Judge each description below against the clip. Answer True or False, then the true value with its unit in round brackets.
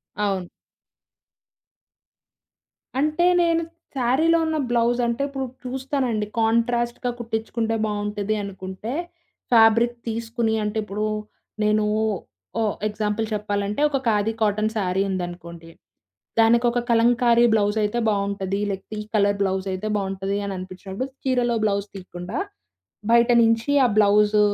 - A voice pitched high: True (215 Hz)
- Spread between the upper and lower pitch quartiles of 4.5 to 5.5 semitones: False (2.9 semitones)